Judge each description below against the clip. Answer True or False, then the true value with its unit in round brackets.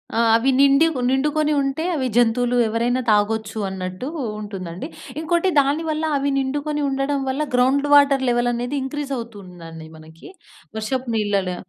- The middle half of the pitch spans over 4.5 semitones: True (5.0 semitones)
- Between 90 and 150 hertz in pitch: False (255 Hz)